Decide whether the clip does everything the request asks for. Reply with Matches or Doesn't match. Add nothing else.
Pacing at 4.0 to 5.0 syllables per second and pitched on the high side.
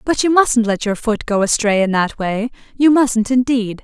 Matches